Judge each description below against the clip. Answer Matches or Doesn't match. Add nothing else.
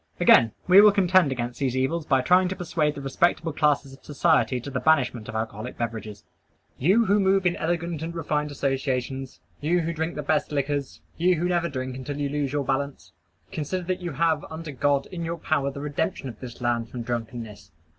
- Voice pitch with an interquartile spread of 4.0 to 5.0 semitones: Matches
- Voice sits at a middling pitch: Matches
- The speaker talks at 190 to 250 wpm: Matches